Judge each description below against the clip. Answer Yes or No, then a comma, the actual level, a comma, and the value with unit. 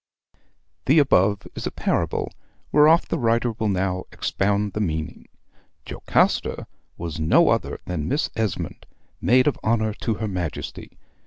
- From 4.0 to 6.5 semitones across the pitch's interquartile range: Yes, average, 4.5 semitones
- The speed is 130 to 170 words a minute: Yes, average, 140 wpm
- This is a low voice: Yes, low, 105 Hz